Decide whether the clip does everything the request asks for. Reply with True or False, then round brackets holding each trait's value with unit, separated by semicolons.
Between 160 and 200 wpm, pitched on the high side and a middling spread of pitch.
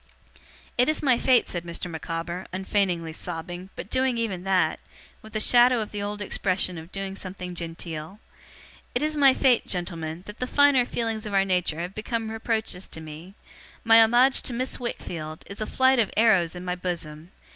True (185 wpm; 195 Hz; 4.9 semitones)